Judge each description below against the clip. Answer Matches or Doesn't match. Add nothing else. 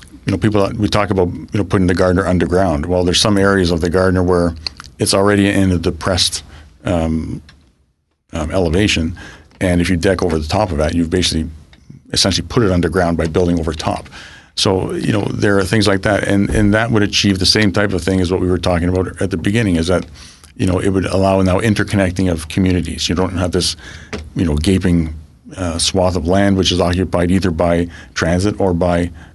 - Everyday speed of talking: Doesn't match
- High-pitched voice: Doesn't match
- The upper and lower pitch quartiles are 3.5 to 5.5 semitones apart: Doesn't match